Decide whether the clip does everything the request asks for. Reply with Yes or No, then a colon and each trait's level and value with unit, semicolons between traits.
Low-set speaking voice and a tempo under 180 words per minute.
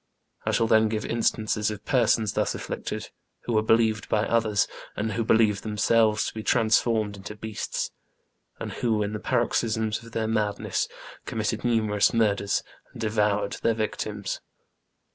Yes: low, 110 Hz; average, 150 wpm